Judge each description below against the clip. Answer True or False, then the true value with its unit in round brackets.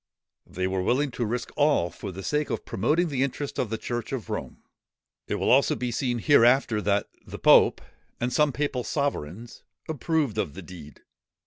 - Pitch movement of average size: False (6.0 semitones)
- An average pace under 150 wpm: False (185 wpm)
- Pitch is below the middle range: True (120 Hz)